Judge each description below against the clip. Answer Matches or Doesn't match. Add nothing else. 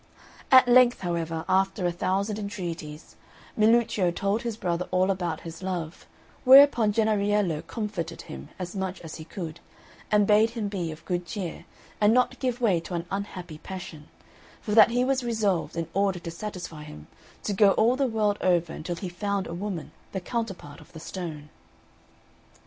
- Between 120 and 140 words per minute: Doesn't match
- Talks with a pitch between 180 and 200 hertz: Matches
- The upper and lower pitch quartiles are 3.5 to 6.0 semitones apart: Matches